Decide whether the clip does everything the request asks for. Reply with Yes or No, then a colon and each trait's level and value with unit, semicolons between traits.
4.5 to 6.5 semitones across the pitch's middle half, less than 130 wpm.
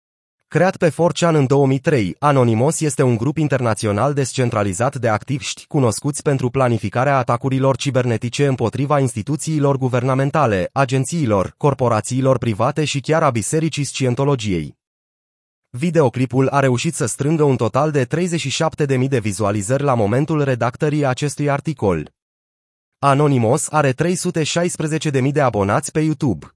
No: average, 3.7 semitones; average, 120 wpm